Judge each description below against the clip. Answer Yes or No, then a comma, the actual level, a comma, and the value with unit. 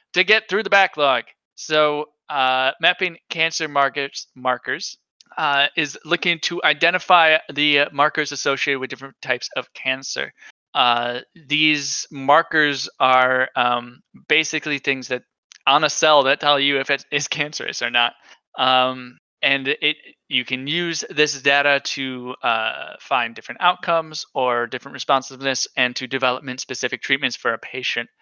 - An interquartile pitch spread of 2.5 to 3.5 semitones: Yes, average, 2.9 semitones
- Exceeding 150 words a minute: No, average, 145 wpm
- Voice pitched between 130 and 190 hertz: Yes, medium, 140 Hz